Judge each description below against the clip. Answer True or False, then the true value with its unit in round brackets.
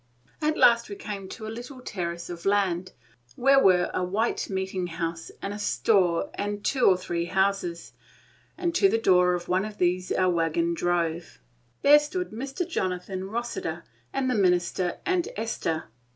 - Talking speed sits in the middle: True (165 wpm)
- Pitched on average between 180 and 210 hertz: True (190 Hz)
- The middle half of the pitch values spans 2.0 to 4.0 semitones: False (4.9 semitones)